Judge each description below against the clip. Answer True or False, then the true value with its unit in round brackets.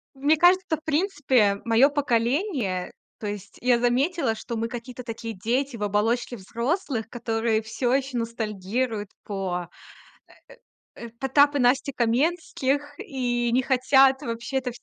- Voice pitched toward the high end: True (245 Hz)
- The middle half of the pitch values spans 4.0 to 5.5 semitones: False (3.4 semitones)